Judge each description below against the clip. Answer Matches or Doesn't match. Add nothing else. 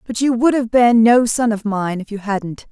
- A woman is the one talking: Matches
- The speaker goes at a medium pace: Doesn't match